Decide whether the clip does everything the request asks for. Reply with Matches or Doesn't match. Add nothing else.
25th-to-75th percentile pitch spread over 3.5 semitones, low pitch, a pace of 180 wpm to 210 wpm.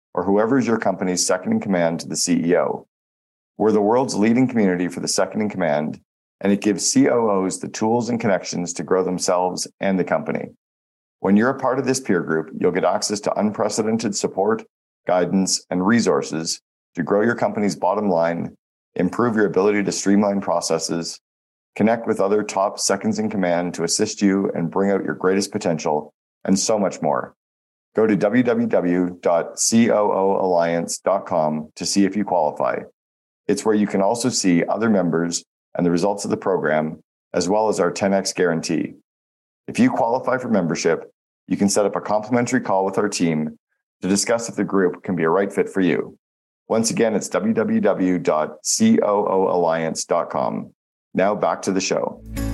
Doesn't match